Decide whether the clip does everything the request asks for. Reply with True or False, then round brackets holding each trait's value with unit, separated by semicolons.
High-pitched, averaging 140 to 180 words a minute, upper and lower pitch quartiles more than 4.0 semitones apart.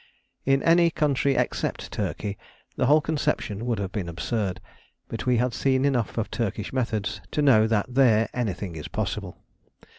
False (115 Hz; 160 wpm; 4.7 semitones)